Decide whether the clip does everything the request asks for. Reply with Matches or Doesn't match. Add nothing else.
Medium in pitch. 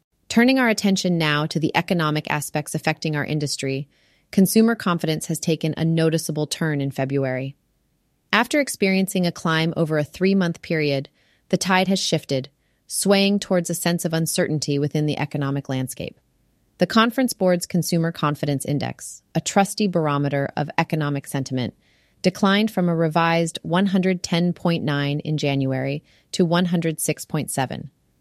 Matches